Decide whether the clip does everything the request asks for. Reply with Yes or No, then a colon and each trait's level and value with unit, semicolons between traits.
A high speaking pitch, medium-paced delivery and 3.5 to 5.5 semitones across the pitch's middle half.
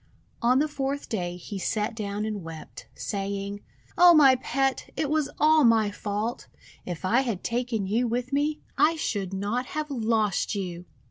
Yes: high, 225 Hz; average, 175 wpm; average, 5.2 semitones